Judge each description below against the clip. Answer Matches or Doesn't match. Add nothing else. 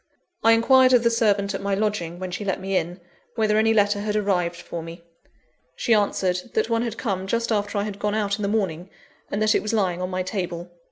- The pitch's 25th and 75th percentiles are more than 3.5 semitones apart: Doesn't match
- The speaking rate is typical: Doesn't match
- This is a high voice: Matches